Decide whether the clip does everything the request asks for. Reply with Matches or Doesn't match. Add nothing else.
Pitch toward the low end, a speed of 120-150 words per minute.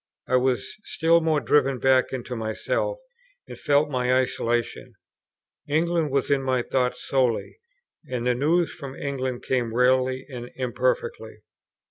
Matches